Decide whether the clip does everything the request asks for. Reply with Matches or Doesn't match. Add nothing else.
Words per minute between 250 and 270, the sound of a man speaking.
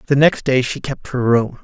Matches